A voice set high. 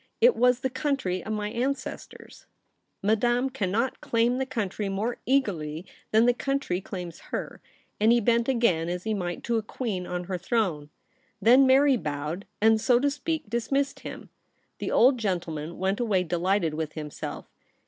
Yes: high, 220 Hz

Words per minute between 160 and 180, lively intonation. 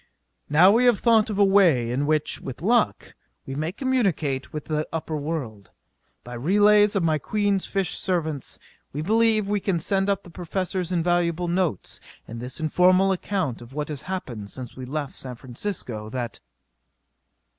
Yes: average, 165 wpm; wide, 6.2 semitones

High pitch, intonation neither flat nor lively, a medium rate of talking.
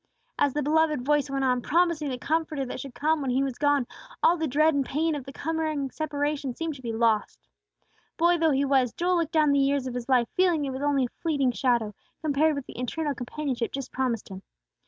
No: very high, 280 Hz; average, 3.3 semitones; fast, 225 wpm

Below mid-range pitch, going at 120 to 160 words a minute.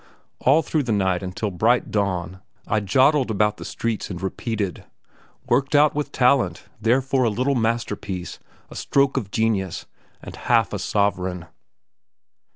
Yes: low, 110 Hz; average, 150 wpm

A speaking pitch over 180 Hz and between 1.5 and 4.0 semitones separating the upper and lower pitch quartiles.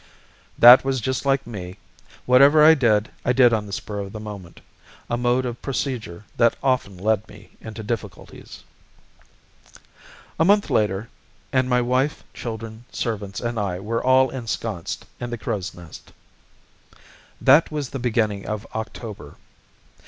No: low, 115 Hz; average, 3.5 semitones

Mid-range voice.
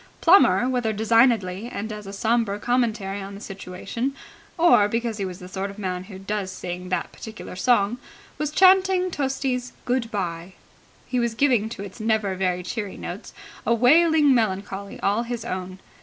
No: high, 215 Hz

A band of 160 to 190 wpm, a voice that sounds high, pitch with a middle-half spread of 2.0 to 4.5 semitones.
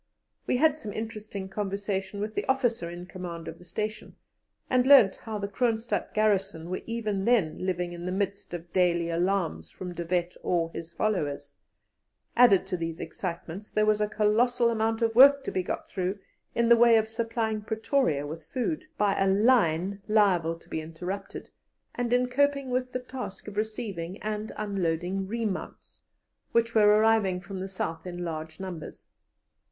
Yes: average, 170 wpm; high, 200 Hz; average, 4.2 semitones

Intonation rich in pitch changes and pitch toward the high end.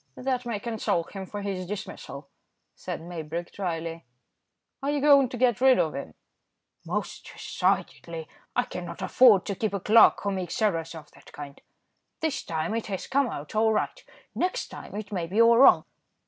Yes: wide, 5.9 semitones; high, 200 Hz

